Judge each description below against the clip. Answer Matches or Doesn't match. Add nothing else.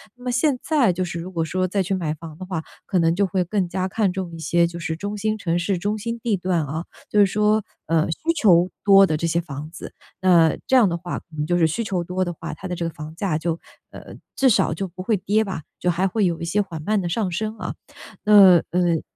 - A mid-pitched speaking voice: Matches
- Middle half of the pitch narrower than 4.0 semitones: Matches